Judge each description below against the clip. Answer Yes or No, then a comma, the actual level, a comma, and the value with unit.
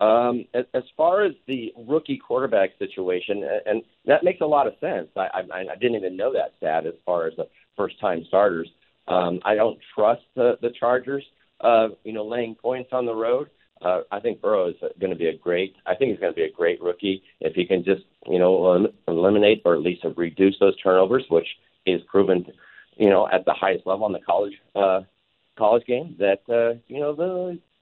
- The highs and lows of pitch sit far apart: Yes, wide, 9.0 semitones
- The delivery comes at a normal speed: No, fast, 210 wpm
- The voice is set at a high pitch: No, low, 120 Hz